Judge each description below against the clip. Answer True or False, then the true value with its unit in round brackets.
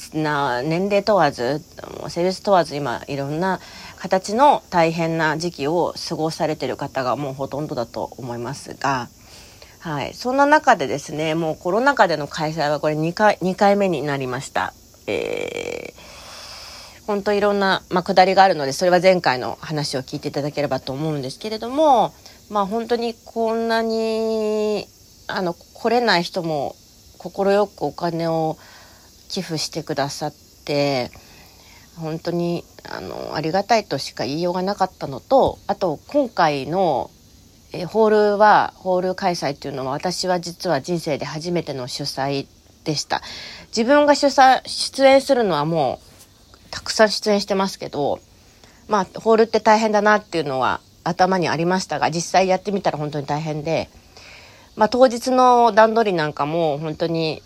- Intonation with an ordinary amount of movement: False (6.2 semitones)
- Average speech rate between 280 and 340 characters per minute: True (310 characters per minute)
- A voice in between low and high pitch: True (170 Hz)